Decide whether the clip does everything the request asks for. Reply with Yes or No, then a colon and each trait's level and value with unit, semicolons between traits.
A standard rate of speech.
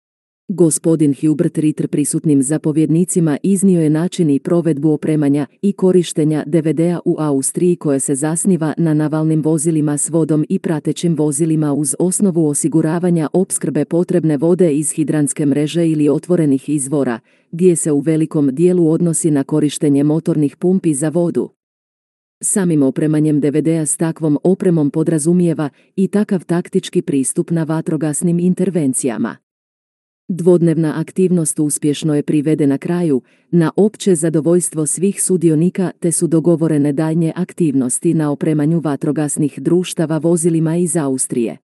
Yes: average, 125 wpm